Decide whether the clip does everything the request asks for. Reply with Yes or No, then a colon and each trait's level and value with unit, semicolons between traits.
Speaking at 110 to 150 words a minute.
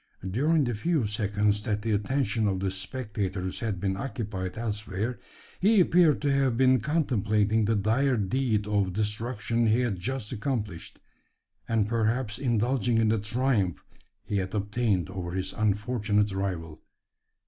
Yes: average, 145 wpm